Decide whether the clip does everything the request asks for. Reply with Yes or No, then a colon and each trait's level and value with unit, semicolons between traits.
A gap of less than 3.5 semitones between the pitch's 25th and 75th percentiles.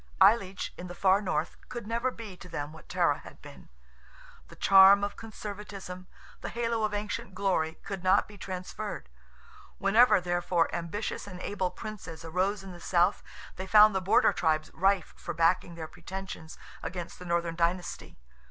Yes: average, 2.8 semitones